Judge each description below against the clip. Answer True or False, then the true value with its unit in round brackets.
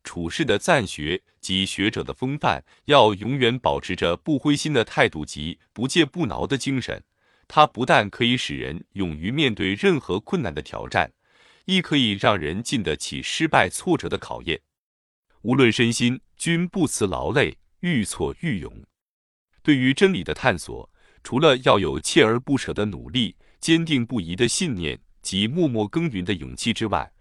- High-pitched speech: False (125 Hz)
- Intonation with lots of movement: True (6.4 semitones)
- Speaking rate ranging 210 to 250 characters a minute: True (245 characters per minute)